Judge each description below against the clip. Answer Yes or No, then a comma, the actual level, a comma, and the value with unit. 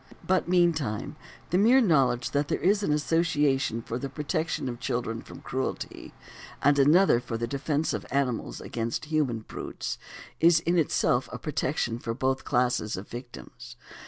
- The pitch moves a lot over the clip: No, average, 4.9 semitones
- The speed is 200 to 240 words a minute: No, average, 160 wpm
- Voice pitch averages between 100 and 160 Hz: Yes, medium, 140 Hz